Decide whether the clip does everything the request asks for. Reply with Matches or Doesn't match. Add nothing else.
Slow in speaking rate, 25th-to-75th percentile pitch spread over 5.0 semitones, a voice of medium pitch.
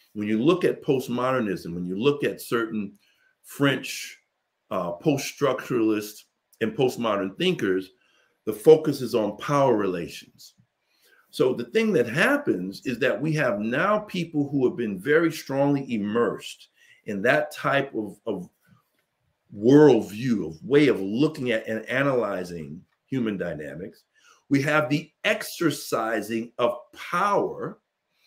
Doesn't match